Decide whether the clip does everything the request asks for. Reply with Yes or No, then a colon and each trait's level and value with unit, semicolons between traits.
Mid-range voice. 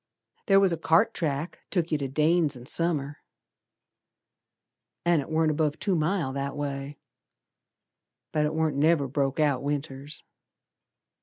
Yes: medium, 150 Hz